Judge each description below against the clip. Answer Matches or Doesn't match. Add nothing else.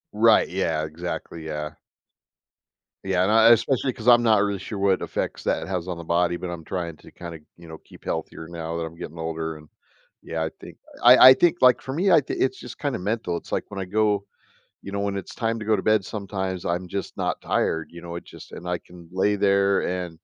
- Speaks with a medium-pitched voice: Doesn't match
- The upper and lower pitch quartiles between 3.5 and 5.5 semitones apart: Matches